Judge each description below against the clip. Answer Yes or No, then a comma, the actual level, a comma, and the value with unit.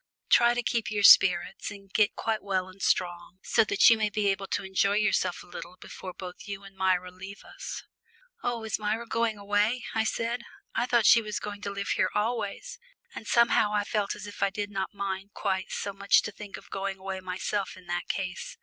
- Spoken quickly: Yes, fast, 220 wpm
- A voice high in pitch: Yes, high, 200 Hz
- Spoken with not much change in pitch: Yes, narrow, 2.1 semitones